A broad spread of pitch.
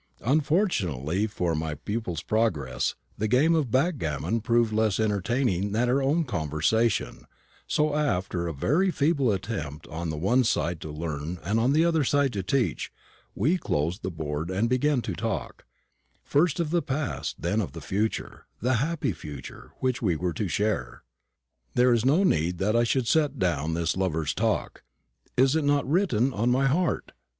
Yes: wide, 8.1 semitones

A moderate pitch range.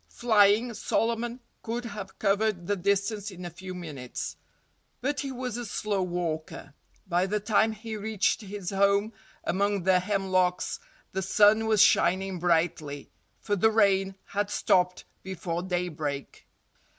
Yes: average, 3.1 semitones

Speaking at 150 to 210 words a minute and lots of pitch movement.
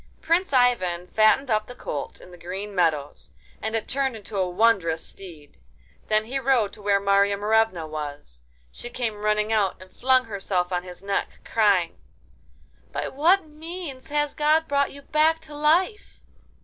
Yes: average, 165 wpm; wide, 6.8 semitones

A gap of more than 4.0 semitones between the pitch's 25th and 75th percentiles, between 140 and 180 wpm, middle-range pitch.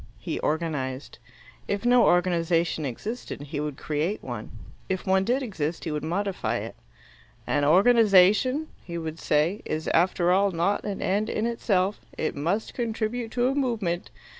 Yes: wide, 5.4 semitones; average, 155 wpm; medium, 180 Hz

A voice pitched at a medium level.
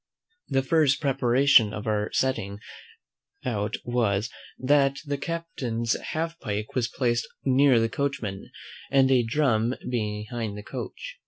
No: low, 125 Hz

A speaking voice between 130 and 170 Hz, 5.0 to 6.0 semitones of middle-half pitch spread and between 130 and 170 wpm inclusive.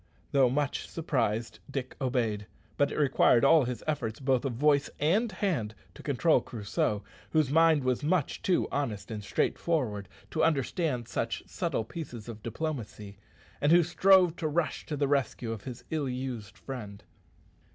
Yes: low, 135 Hz; average, 5.3 semitones; average, 160 wpm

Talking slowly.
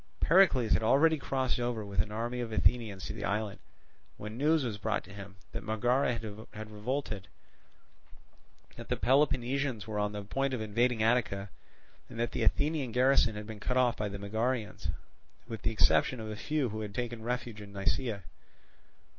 No: average, 180 wpm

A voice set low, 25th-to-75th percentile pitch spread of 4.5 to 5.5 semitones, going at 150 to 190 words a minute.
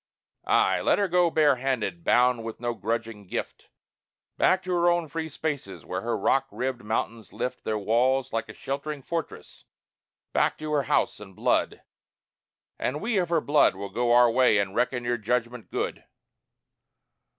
Yes: low, 125 Hz; average, 5.1 semitones; average, 170 wpm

